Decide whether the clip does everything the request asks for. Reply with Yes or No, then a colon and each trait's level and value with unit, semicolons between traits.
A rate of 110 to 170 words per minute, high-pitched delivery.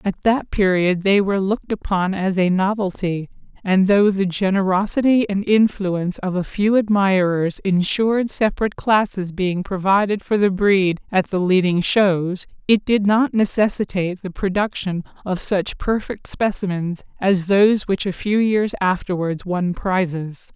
Yes: average, 150 wpm; high, 195 Hz